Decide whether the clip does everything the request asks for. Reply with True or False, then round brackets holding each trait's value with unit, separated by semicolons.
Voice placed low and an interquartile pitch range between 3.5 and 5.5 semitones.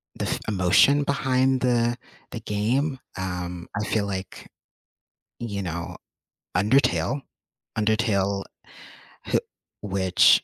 True (105 Hz; 5.1 semitones)